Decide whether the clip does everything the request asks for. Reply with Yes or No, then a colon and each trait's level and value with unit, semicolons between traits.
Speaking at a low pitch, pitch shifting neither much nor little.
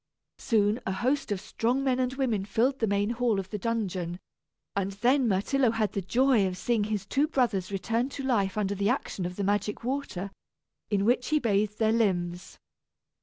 No: high, 215 Hz; average, 4.0 semitones